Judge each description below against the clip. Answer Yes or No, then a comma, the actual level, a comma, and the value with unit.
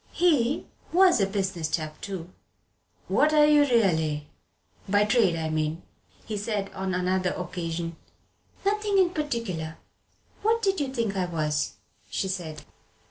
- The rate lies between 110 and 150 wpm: Yes, slow, 135 wpm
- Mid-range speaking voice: No, high, 195 Hz